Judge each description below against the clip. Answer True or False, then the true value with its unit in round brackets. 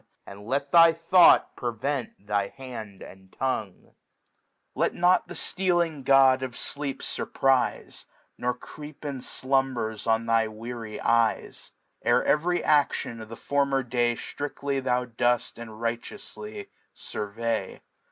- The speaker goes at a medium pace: False (125 wpm)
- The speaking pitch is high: False (125 Hz)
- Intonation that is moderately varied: True (3.8 semitones)